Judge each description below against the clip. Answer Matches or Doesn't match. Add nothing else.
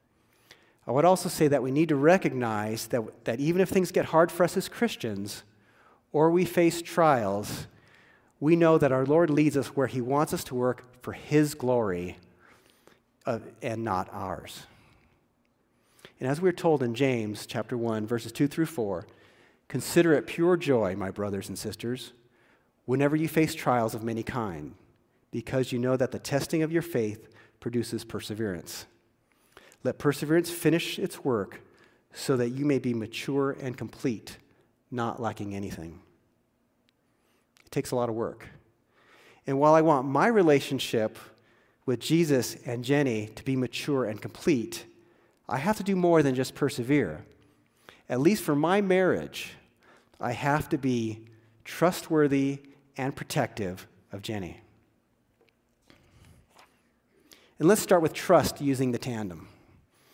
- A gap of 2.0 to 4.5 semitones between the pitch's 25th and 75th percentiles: Doesn't match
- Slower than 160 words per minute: Matches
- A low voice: Matches